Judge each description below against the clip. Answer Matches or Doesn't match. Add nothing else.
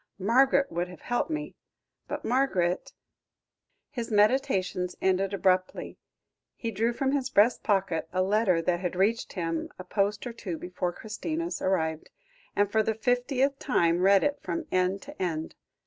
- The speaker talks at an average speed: Matches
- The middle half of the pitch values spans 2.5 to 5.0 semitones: Doesn't match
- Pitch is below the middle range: Doesn't match